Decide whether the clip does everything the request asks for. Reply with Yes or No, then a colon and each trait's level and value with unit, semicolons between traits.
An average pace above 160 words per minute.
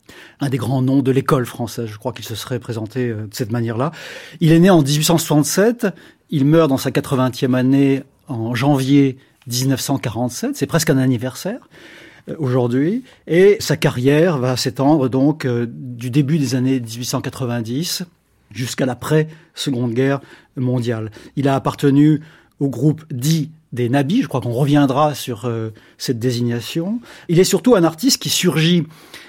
No: average, 150 wpm